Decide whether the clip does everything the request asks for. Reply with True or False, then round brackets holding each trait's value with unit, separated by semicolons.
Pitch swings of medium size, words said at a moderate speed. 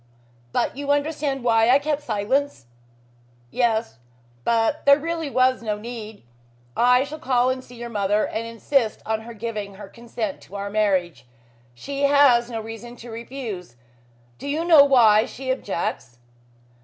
True (4.3 semitones; 155 wpm)